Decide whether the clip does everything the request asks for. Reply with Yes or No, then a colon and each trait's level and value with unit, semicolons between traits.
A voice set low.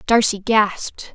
No: high, 210 Hz